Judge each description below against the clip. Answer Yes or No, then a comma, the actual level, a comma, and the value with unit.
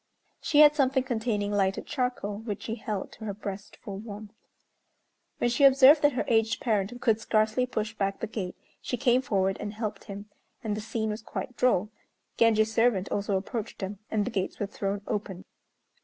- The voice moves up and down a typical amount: Yes, average, 3.0 semitones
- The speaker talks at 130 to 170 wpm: No, average, 185 wpm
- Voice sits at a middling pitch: No, high, 215 Hz